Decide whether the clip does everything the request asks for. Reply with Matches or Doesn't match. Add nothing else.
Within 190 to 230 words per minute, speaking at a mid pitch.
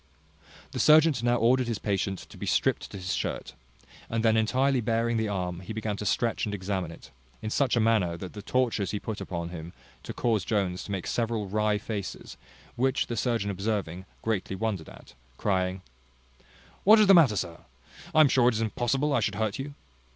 Doesn't match